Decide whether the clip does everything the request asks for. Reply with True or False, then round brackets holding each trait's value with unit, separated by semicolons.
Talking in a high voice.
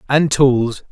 False (135 Hz)